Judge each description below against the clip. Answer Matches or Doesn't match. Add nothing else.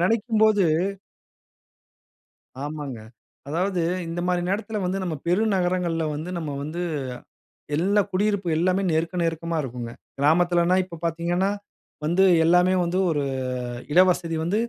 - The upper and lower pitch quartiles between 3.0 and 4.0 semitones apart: Doesn't match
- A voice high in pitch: Doesn't match